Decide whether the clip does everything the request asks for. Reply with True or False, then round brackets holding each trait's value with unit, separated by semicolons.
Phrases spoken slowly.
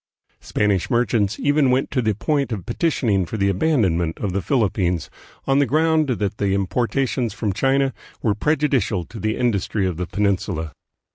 False (170 wpm)